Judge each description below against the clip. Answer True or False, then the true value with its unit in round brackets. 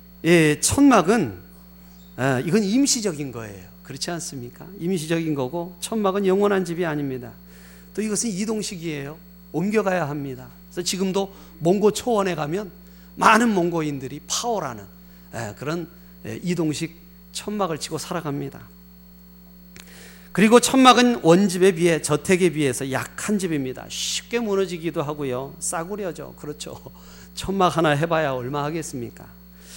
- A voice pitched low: False (165 Hz)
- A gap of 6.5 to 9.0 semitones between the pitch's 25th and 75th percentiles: True (6.8 semitones)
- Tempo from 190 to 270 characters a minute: False (305 characters per minute)